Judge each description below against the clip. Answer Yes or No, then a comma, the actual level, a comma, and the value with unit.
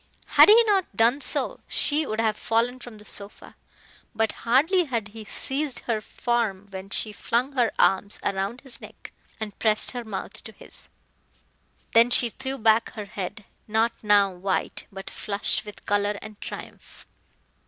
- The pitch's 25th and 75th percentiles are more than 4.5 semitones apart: No, average, 3.2 semitones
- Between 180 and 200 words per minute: No, average, 165 wpm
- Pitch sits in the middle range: No, high, 220 Hz